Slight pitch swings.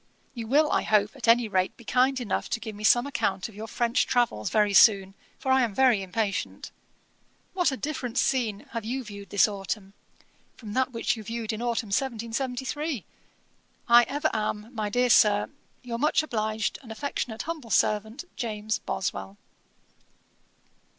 No: average, 3.4 semitones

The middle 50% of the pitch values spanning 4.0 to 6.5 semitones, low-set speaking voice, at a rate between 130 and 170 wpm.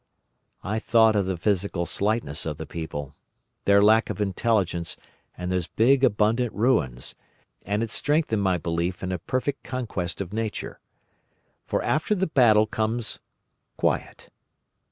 Yes: average, 4.3 semitones; low, 105 Hz; average, 140 wpm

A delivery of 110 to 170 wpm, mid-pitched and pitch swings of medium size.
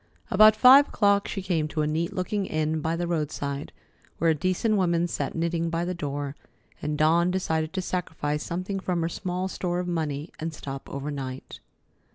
No: average, 185 wpm; medium, 170 Hz; average, 3.2 semitones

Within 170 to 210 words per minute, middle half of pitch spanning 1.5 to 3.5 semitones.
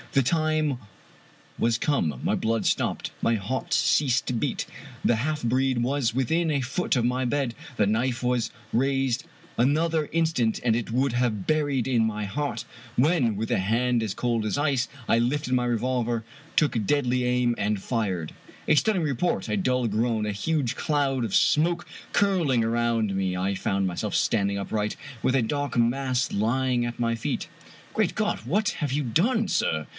No: average, 180 wpm; average, 4.0 semitones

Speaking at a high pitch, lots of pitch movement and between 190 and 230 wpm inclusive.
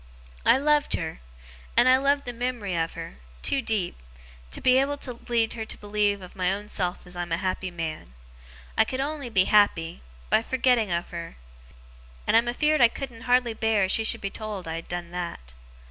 Yes: high, 215 Hz; wide, 5.8 semitones; average, 200 wpm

